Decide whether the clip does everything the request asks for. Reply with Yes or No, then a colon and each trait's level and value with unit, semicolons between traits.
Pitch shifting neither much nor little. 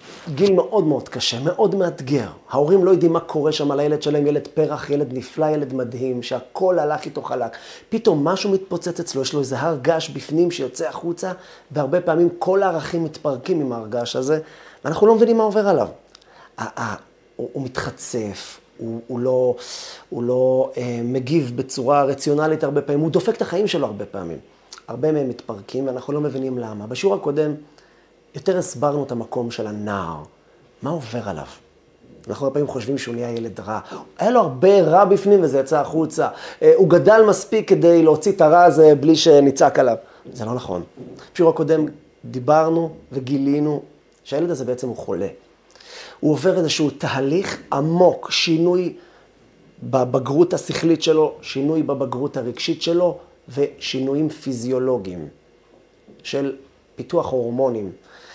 Yes: average, 4.9 semitones